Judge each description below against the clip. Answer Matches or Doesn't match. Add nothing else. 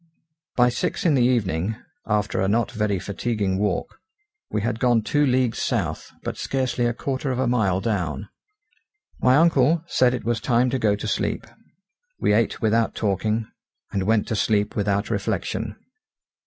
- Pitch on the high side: Doesn't match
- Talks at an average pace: Matches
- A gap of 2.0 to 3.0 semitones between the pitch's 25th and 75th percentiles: Doesn't match